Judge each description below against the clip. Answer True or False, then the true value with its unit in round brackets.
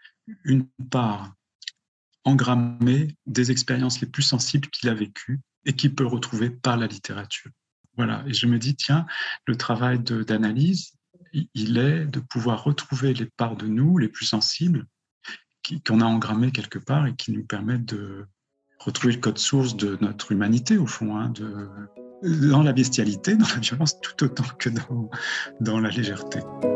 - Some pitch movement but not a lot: True (3.7 semitones)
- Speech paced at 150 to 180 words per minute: True (170 wpm)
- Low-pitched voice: True (125 Hz)